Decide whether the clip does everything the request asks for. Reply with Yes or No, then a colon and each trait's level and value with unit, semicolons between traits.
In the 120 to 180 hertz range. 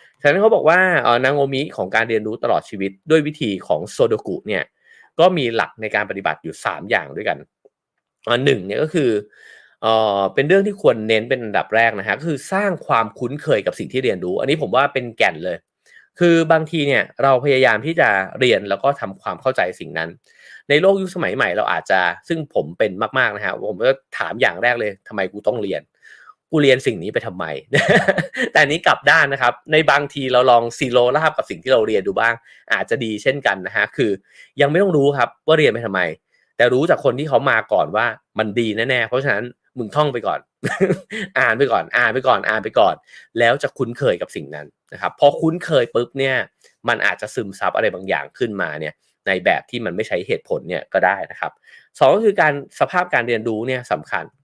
Yes: medium, 140 Hz